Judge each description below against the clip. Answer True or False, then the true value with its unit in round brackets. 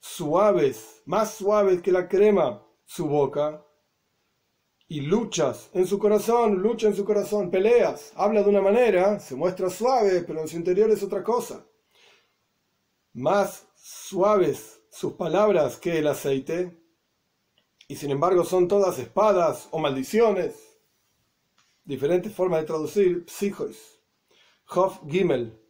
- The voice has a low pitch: False (190 Hz)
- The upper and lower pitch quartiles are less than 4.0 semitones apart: False (4.3 semitones)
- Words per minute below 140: True (125 wpm)